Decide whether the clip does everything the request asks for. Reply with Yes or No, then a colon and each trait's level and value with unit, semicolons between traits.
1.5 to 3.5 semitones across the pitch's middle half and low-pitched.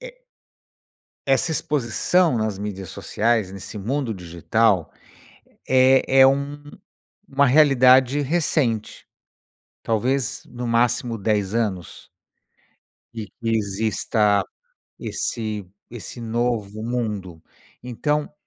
No: average, 4.2 semitones; low, 115 Hz